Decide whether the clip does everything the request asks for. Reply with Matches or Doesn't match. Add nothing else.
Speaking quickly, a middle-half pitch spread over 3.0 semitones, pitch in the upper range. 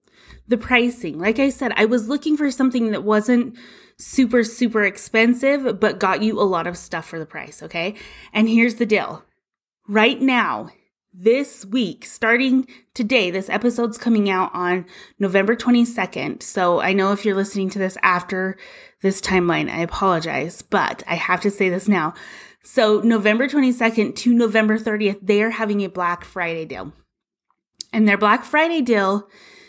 Doesn't match